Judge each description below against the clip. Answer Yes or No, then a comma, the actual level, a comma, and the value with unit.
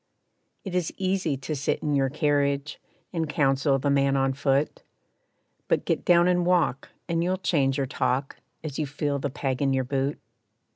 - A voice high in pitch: No, medium, 140 Hz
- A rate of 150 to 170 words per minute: No, average, 180 wpm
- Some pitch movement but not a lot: Yes, average, 3.0 semitones